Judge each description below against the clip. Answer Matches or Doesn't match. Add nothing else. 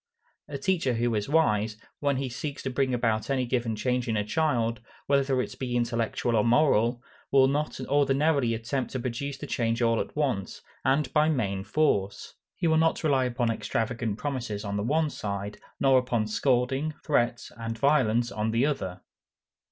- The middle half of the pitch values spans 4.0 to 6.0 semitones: Doesn't match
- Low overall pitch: Matches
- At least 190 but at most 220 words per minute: Doesn't match